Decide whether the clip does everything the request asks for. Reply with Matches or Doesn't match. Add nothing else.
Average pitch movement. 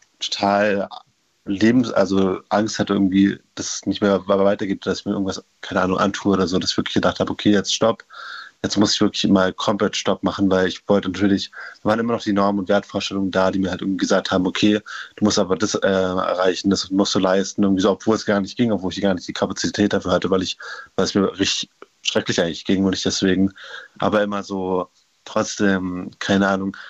Doesn't match